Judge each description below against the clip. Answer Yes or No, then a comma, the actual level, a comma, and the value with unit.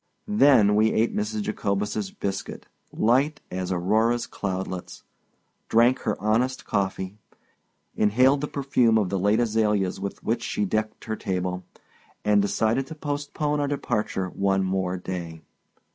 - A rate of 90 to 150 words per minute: Yes, slow, 135 wpm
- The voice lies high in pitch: No, low, 105 Hz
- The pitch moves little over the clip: No, average, 3.9 semitones